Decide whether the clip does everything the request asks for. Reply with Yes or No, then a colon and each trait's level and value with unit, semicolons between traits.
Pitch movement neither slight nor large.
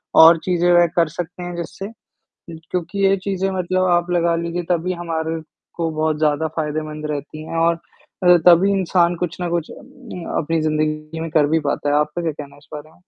No: narrow, 2.2 semitones